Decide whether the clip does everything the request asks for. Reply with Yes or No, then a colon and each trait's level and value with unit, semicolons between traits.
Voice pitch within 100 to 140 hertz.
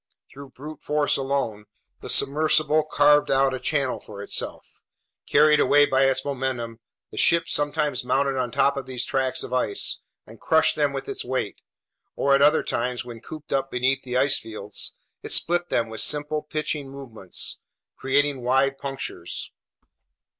Yes: low, 135 Hz